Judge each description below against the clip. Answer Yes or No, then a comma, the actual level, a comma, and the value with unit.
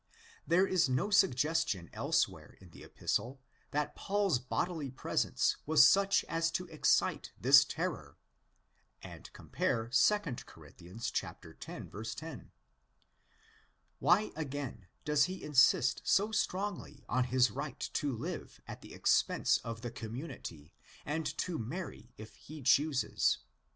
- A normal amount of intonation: No, wide, 6.4 semitones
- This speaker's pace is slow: Yes, slow, 125 wpm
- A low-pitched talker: No, medium, 145 Hz